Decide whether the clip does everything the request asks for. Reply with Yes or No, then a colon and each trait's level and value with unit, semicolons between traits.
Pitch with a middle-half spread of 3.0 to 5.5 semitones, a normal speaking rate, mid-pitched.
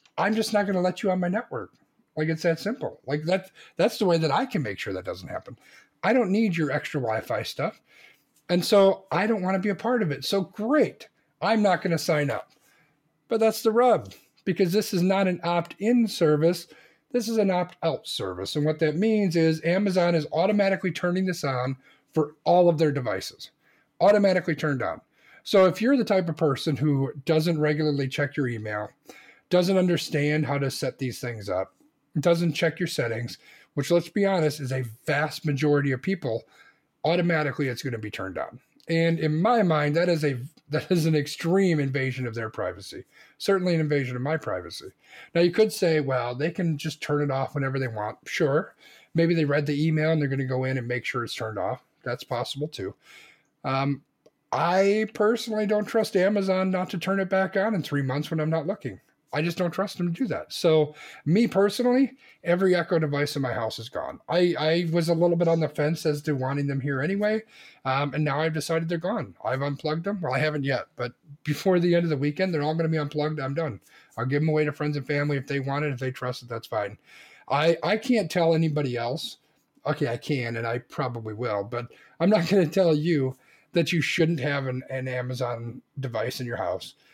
No: average, 4.7 semitones; fast, 220 wpm; medium, 155 Hz